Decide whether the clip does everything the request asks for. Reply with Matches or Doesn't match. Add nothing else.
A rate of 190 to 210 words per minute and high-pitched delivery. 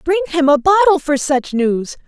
Matches